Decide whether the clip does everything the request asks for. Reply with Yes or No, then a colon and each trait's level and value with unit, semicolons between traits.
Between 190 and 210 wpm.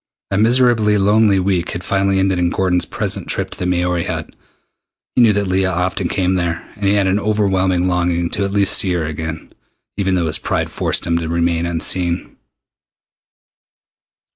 No: average, 180 wpm